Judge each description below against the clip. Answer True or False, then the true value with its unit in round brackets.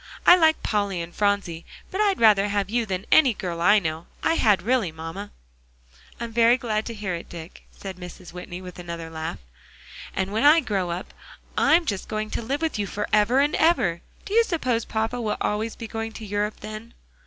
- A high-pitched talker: True (210 Hz)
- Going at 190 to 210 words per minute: True (200 wpm)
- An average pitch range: True (4.4 semitones)